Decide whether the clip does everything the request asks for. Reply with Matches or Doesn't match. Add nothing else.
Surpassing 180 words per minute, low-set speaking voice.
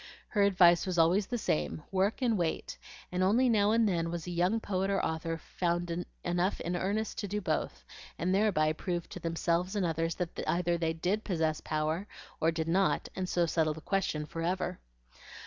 Doesn't match